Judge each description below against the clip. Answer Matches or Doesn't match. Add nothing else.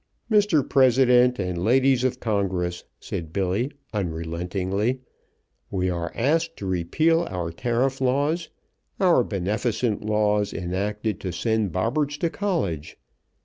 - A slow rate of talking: Matches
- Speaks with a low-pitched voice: Matches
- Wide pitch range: Matches